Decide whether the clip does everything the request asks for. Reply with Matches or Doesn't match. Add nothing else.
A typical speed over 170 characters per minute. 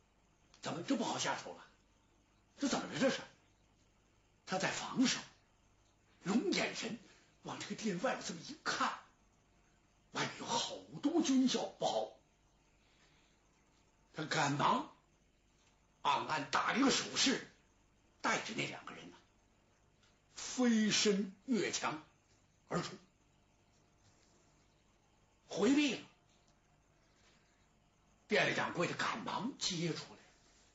Doesn't match